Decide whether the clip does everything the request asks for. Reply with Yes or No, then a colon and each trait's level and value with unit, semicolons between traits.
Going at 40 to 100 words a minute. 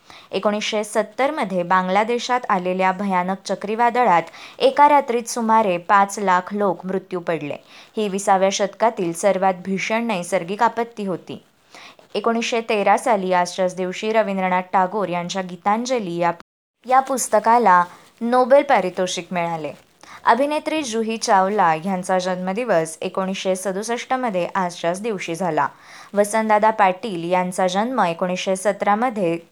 No: average, 115 wpm